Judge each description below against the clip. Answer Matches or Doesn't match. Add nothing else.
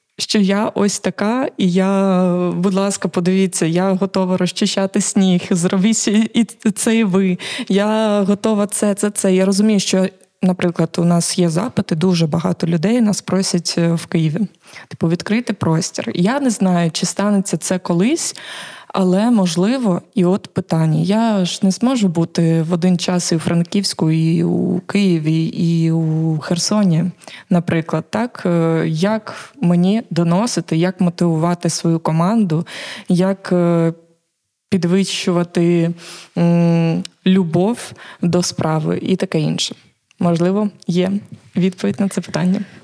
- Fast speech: Doesn't match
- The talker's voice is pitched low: Doesn't match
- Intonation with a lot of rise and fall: Doesn't match